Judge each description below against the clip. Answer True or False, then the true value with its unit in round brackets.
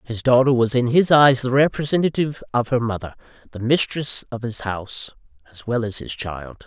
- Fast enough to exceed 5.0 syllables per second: True (5.3 syllables/s)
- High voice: False (120 Hz)